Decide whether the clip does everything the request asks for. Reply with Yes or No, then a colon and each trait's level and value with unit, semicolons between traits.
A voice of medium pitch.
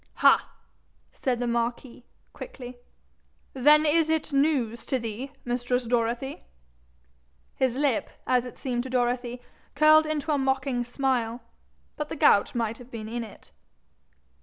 No: very high, 250 Hz